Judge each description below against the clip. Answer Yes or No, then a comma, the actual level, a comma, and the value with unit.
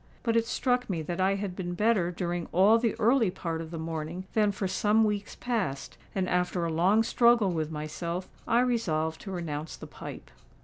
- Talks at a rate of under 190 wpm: No, average, 195 wpm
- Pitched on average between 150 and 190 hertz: Yes, medium, 185 Hz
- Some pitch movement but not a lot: Yes, average, 4.8 semitones